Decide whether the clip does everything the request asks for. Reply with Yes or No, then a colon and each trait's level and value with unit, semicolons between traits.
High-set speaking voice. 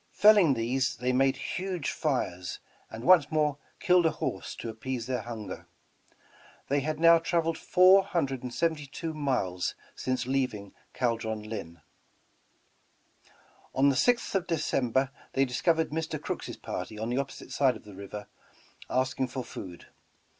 No: low, 135 Hz